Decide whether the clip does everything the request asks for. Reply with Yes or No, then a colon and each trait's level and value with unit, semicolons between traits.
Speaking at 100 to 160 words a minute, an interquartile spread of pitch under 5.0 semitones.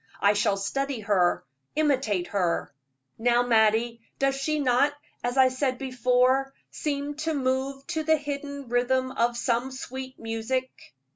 Yes: average, 140 wpm; average, 2.9 semitones